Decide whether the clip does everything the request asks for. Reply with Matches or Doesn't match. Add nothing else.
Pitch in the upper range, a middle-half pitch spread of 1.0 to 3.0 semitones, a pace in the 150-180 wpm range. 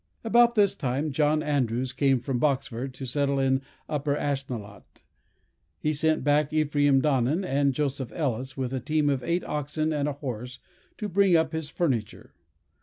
Doesn't match